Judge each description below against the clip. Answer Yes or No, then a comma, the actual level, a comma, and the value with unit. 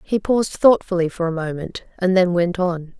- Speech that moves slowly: No, average, 200 wpm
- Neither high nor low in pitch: Yes, medium, 180 Hz